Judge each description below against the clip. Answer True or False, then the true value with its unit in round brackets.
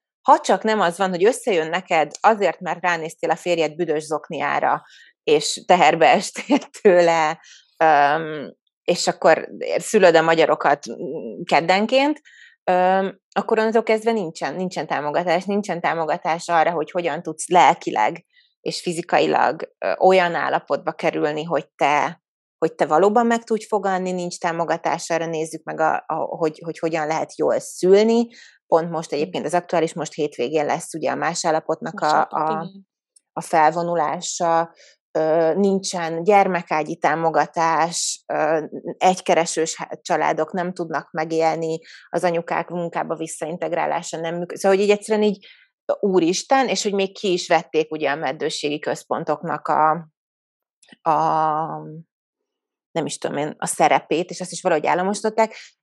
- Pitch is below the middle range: False (170 Hz)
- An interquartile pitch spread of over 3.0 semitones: True (3.5 semitones)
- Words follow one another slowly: False (130 wpm)